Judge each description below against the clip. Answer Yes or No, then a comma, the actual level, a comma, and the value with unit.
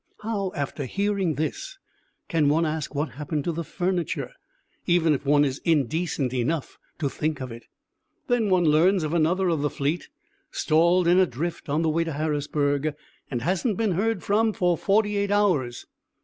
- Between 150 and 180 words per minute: Yes, average, 175 wpm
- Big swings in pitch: No, average, 4.2 semitones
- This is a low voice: No, medium, 165 Hz